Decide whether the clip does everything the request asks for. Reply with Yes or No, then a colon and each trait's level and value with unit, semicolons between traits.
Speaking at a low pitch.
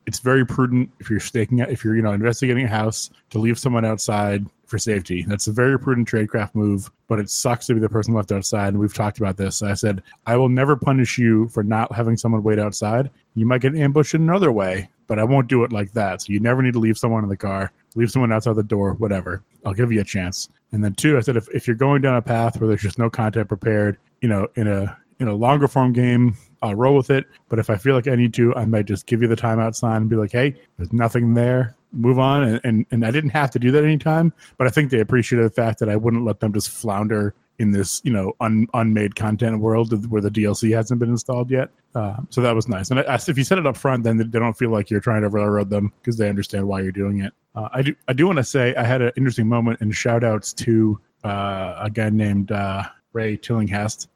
Yes: low, 115 Hz